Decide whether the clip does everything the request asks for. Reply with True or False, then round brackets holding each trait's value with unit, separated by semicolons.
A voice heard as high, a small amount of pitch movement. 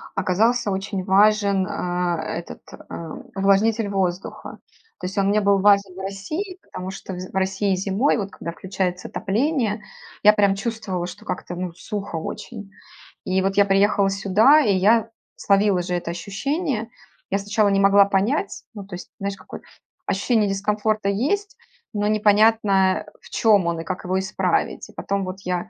True (195 Hz; 2.0 semitones)